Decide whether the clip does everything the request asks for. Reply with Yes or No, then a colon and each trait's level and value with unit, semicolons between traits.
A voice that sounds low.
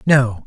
Yes: low, 125 Hz